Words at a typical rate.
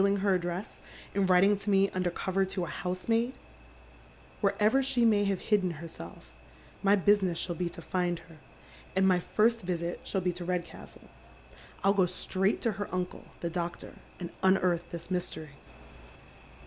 Yes: average, 160 wpm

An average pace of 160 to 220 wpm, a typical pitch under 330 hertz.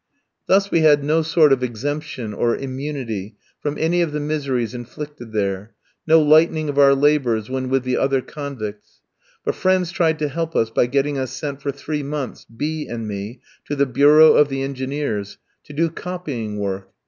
Yes: average, 185 wpm; medium, 140 Hz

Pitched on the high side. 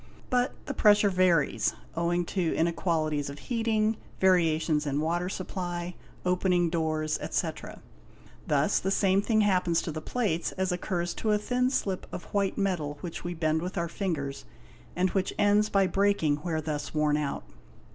No: medium, 175 Hz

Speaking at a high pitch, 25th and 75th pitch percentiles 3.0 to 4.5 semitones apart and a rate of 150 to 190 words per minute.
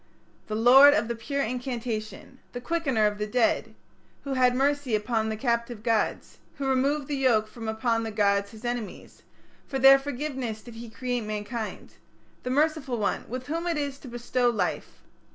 Yes: high, 245 Hz; average, 3.4 semitones; average, 180 wpm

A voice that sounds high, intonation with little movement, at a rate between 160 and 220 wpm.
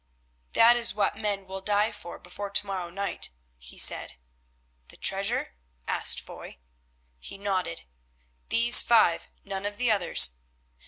No: high, 200 Hz; narrow, 2.1 semitones; average, 140 wpm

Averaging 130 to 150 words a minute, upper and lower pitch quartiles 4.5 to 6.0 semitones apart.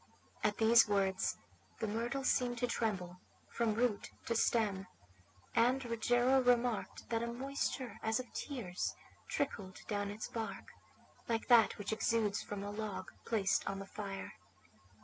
No: average, 145 wpm; average, 2.9 semitones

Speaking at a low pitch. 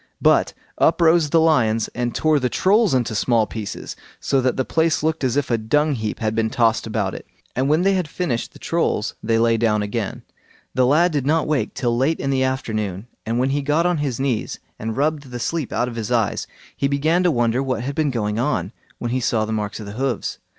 Yes: low, 130 Hz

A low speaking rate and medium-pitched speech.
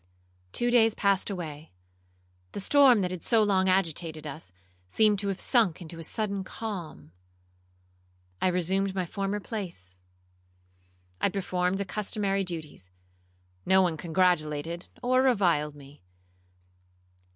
Yes: slow, 115 wpm; medium, 175 Hz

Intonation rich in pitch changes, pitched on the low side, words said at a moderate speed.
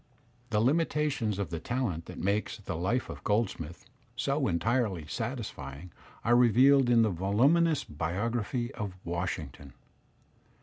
No: wide, 5.7 semitones; low, 110 Hz; slow, 130 wpm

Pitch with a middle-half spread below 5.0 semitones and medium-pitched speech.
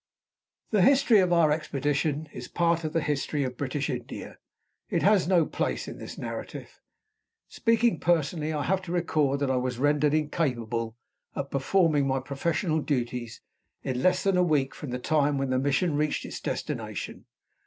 Yes: average, 3.9 semitones; medium, 150 Hz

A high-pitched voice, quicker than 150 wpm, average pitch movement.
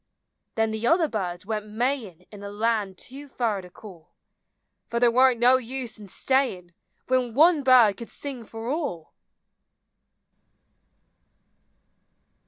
No: high, 230 Hz; slow, 135 wpm; average, 4.0 semitones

